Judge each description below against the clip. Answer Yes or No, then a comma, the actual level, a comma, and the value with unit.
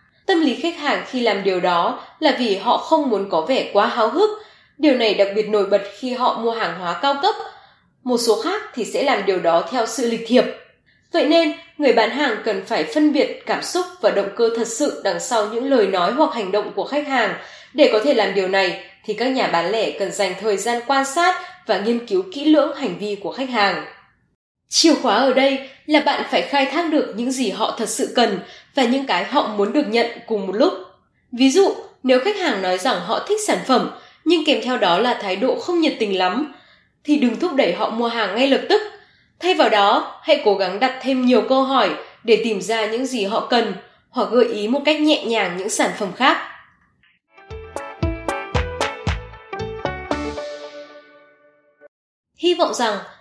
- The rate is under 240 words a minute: Yes, average, 210 wpm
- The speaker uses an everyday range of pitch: No, wide, 6.4 semitones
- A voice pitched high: Yes, high, 240 Hz